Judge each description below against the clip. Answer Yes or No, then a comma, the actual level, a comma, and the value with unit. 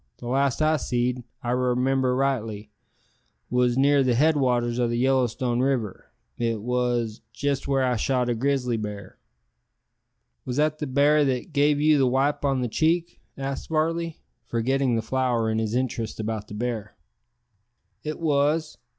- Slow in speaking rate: No, average, 160 wpm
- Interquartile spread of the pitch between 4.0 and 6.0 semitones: No, average, 2.9 semitones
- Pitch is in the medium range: No, low, 130 Hz